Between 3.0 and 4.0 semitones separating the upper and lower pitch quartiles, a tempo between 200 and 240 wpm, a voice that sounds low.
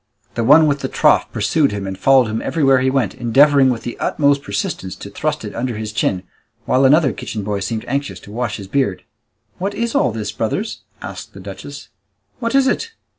No: average, 5.2 semitones; fast, 205 wpm; low, 125 Hz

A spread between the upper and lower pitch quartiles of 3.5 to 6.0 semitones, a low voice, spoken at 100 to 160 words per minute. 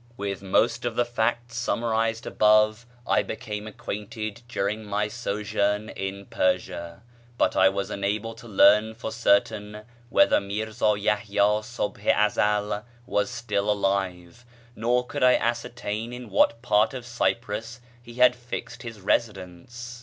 No: narrow, 2.5 semitones; low, 105 Hz; average, 140 wpm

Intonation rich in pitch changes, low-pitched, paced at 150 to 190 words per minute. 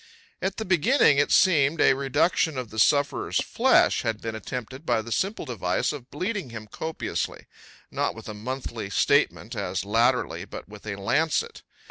Yes: wide, 6.4 semitones; low, 130 Hz; average, 165 wpm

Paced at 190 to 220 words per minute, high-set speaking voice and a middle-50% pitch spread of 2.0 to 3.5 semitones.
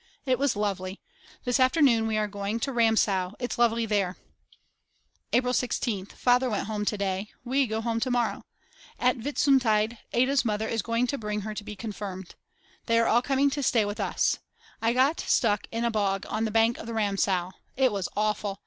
Yes: average, 195 wpm; high, 225 Hz; average, 3.1 semitones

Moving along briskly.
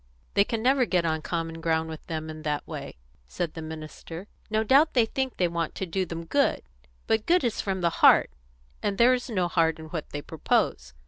Yes: fast, 215 wpm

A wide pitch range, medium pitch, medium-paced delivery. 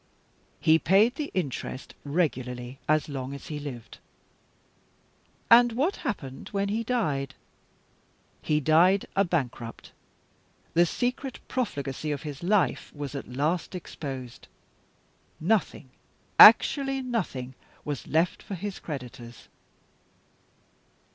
No: wide, 7.1 semitones; medium, 155 Hz; slow, 110 wpm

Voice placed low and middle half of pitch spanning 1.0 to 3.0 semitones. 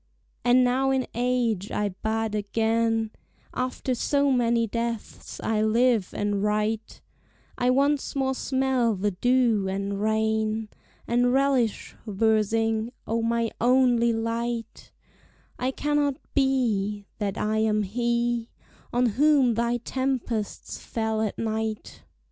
No: high, 230 Hz; narrow, 2.4 semitones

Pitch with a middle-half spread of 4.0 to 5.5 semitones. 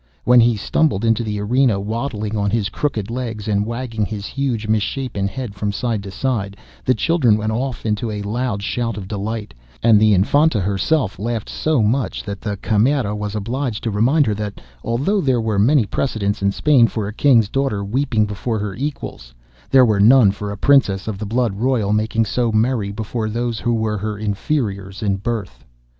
No: average, 3.3 semitones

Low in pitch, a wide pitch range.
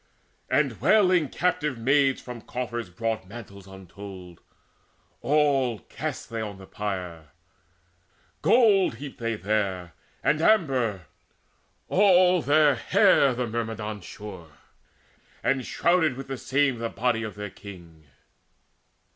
Yes: low, 115 Hz; wide, 6.1 semitones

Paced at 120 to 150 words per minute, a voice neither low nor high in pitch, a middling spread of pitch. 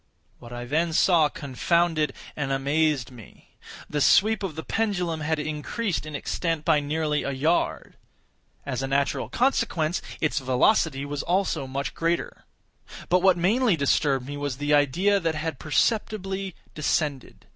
Yes: average, 145 wpm; medium, 155 Hz; average, 3.7 semitones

